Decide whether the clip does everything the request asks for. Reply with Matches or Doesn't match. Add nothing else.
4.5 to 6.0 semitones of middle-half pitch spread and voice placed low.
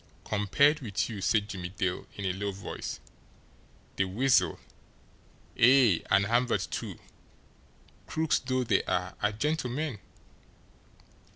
Matches